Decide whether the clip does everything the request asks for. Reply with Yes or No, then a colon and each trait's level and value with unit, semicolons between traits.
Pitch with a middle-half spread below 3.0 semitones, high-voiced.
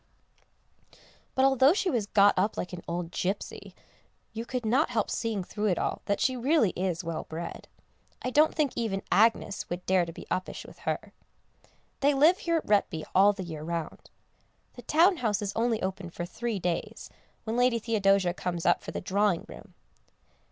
No: average, 5.3 semitones; high, 205 Hz